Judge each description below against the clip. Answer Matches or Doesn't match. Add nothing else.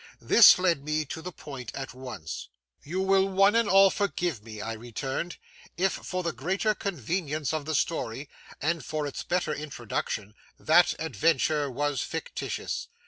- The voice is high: Doesn't match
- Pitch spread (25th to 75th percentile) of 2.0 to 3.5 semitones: Doesn't match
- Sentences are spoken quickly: Doesn't match